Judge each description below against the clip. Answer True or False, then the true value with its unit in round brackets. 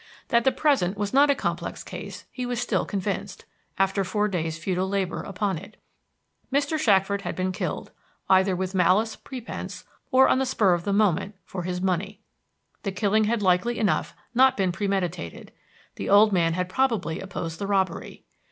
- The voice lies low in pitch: False (195 Hz)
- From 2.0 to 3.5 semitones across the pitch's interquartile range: True (3.0 semitones)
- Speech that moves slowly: False (175 wpm)